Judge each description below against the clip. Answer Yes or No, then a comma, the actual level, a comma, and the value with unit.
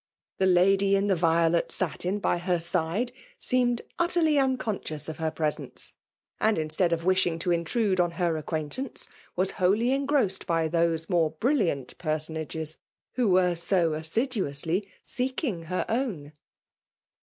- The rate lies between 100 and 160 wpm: Yes, average, 140 wpm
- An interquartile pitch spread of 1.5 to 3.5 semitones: No, average, 5.0 semitones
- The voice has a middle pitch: Yes, medium, 180 Hz